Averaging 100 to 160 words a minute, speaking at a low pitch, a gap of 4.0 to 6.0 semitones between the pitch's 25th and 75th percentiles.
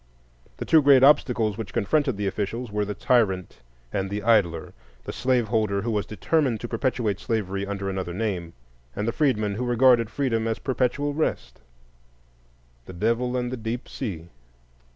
Yes: average, 150 wpm; low, 110 Hz; average, 4.6 semitones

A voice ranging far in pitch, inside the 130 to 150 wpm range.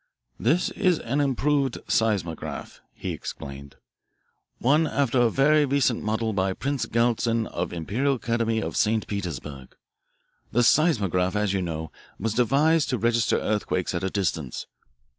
Yes: wide, 6.4 semitones; average, 140 wpm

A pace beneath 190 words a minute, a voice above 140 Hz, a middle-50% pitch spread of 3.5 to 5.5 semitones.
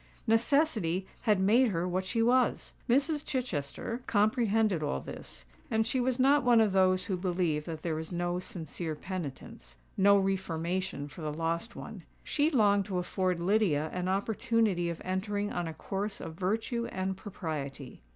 Yes: average, 160 wpm; high, 190 Hz; average, 4.9 semitones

